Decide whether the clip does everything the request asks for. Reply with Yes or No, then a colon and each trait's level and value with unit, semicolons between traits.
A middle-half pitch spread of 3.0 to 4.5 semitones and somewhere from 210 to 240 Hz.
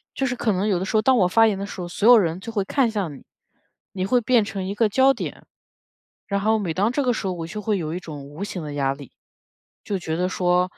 No: average, 4.0 semitones; high, 195 Hz